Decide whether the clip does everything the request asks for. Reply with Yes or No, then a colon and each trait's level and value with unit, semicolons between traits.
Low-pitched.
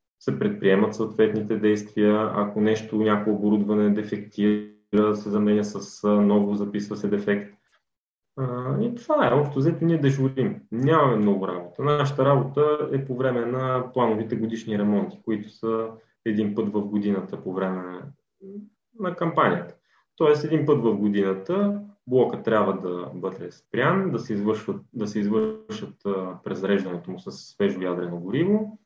Yes: low, 110 Hz